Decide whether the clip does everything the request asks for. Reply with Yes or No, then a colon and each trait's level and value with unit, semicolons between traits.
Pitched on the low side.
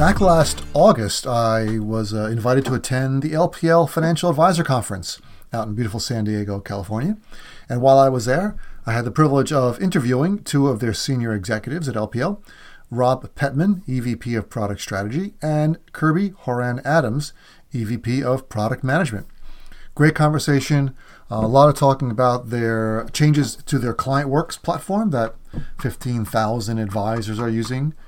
Yes: low, 130 Hz